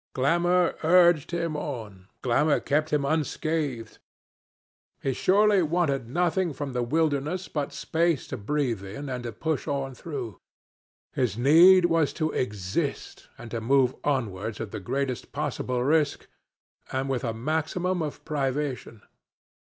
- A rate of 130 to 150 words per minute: Yes, slow, 135 wpm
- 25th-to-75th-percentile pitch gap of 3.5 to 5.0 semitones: Yes, average, 4.6 semitones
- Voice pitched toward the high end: No, medium, 140 Hz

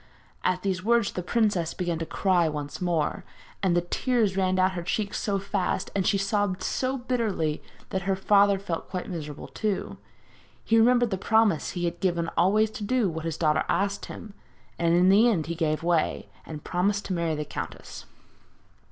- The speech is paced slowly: No, average, 185 wpm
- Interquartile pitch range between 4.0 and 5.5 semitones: No, average, 3.3 semitones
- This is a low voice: No, medium, 185 Hz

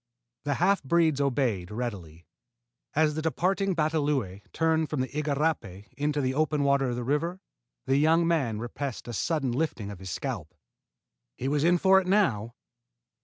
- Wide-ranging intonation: No, average, 5.0 semitones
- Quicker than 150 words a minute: Yes, average, 165 wpm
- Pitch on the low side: No, medium, 145 Hz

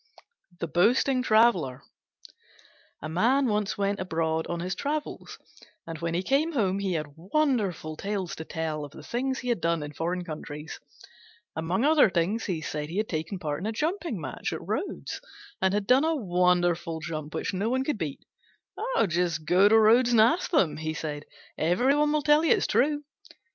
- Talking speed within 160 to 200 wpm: Yes, average, 185 wpm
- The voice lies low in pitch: No, medium, 185 Hz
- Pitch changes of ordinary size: No, wide, 7.1 semitones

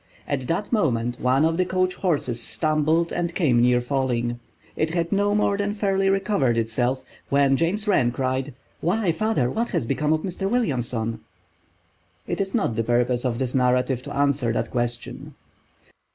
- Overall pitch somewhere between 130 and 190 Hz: Yes, medium, 140 Hz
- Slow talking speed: No, average, 165 wpm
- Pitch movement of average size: No, wide, 7.0 semitones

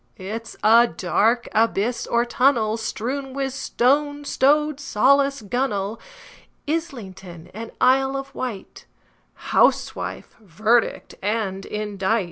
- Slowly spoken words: Yes, slow, 100 wpm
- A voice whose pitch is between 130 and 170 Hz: No, high, 235 Hz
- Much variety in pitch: No, average, 4.4 semitones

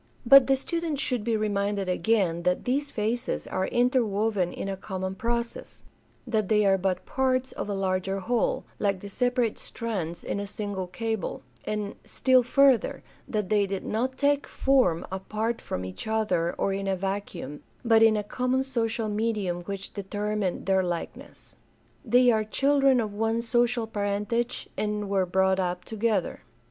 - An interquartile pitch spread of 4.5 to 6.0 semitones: No, average, 3.7 semitones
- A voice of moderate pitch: No, high, 210 Hz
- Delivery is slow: No, average, 160 wpm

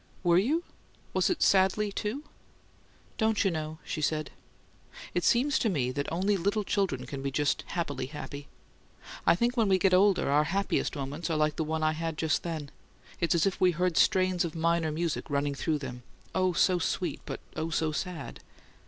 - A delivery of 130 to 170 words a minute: No, average, 190 wpm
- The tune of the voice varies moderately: Yes, average, 3.9 semitones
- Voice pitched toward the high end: No, medium, 170 Hz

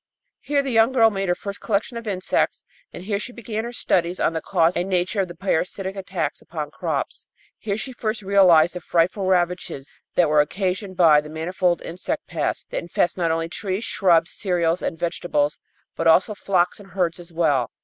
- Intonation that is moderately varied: Yes, average, 3.1 semitones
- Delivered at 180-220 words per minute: Yes, average, 195 wpm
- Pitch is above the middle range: No, medium, 180 Hz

